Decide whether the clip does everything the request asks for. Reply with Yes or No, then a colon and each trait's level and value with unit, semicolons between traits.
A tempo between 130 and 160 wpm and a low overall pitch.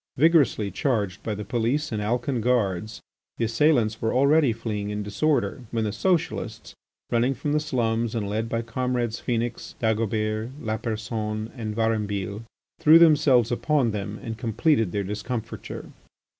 Yes: average, 145 wpm; low, 115 Hz